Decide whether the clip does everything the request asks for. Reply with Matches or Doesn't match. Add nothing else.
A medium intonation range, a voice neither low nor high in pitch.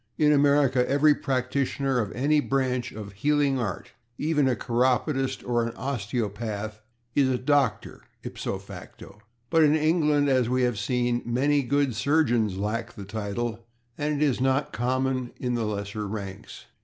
Doesn't match